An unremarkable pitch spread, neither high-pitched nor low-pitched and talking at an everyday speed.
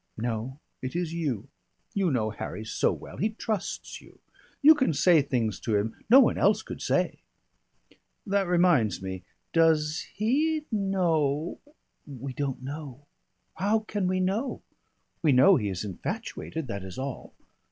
No: wide, 7.8 semitones; medium, 155 Hz; average, 150 wpm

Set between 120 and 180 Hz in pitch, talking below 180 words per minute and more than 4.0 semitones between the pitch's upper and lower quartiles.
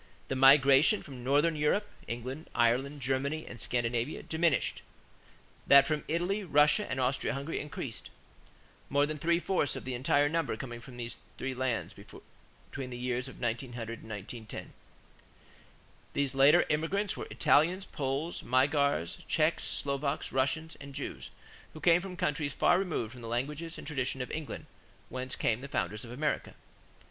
No: medium, 140 Hz; average, 155 wpm; average, 3.6 semitones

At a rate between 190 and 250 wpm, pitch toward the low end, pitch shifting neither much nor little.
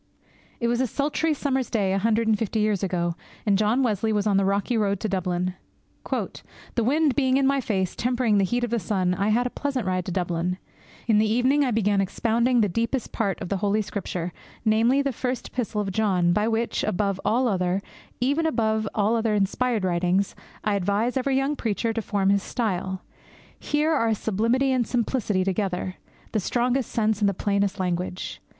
No: average, 195 wpm; high, 215 Hz; average, 3.9 semitones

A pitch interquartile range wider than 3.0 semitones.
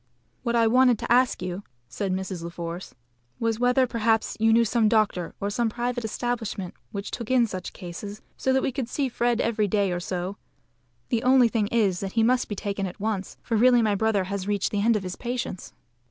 Yes: average, 3.5 semitones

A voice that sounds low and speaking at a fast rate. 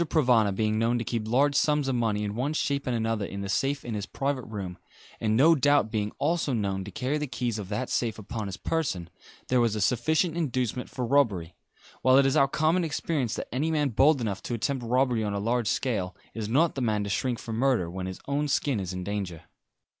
Yes: low, 120 Hz; fast, 230 wpm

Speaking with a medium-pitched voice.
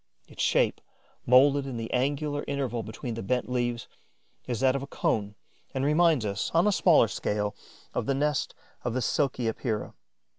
No: low, 130 Hz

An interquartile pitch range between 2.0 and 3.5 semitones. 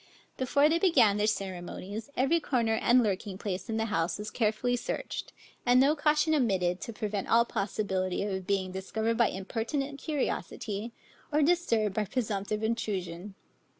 No: average, 4.3 semitones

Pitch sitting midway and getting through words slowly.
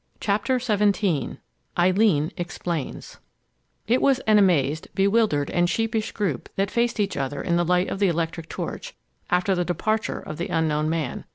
No: medium, 180 Hz; average, 160 wpm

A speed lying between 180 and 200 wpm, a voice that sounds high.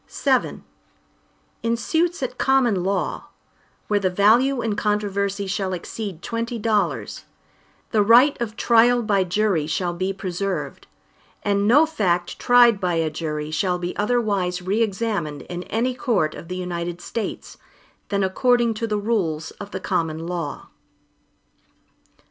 No: average, 140 wpm; high, 200 Hz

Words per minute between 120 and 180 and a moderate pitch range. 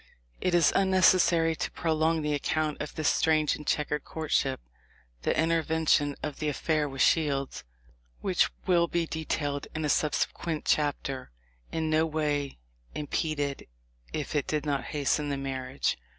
No: average, 150 wpm; narrow, 1.9 semitones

